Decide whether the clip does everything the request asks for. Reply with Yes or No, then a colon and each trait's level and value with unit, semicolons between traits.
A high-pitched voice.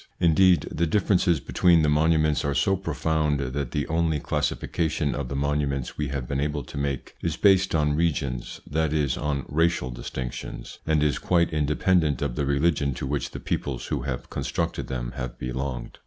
No: very low, 75 Hz